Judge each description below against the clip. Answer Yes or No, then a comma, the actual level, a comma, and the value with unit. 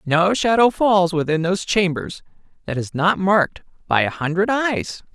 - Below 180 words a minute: Yes, average, 165 wpm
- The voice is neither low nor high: Yes, medium, 180 Hz